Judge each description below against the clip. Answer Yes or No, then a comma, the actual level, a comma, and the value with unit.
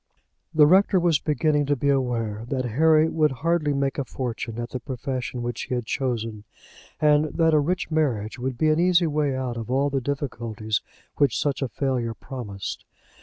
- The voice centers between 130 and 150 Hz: Yes, low, 135 Hz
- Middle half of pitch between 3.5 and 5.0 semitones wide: Yes, average, 4.0 semitones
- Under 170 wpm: No, average, 185 wpm